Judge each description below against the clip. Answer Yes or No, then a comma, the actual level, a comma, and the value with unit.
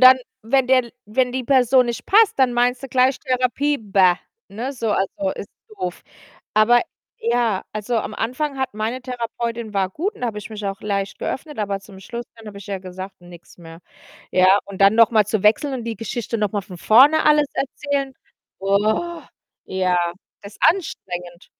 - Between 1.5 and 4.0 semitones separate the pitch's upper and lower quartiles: No, average, 4.4 semitones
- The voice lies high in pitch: Yes, high, 225 Hz